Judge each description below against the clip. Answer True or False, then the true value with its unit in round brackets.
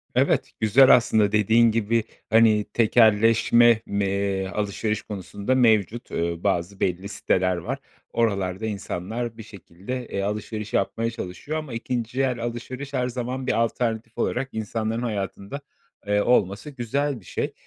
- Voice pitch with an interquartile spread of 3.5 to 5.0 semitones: False (2.9 semitones)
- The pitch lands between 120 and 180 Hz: False (110 Hz)